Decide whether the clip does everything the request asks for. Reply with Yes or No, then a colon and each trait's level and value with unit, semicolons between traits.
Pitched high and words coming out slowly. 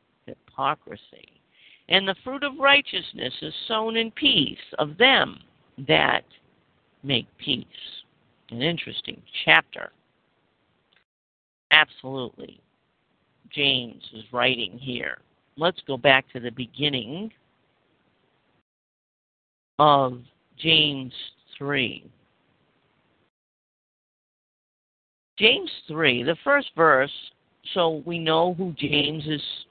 No: medium, 145 Hz; slow, 85 wpm